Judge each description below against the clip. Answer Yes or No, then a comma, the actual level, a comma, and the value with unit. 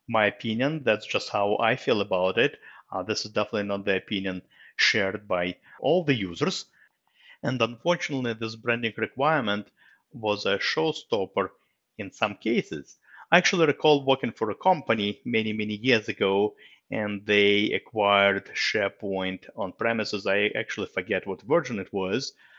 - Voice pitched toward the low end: Yes, low, 105 Hz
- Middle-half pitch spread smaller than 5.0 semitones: Yes, average, 2.8 semitones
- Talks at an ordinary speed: Yes, average, 150 wpm